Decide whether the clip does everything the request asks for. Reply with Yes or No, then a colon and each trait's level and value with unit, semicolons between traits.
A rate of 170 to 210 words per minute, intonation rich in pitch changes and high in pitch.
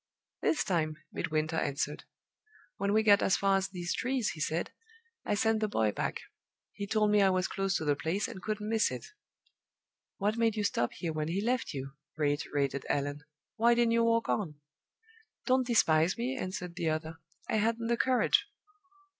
Yes: average, 180 wpm; wide, 6.0 semitones; high, 195 Hz